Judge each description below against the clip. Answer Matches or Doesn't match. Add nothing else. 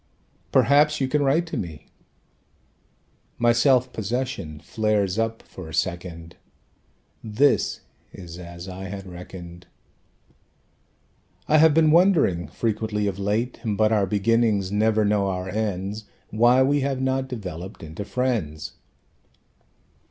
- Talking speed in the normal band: Doesn't match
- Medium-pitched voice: Doesn't match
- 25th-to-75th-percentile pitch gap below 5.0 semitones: Doesn't match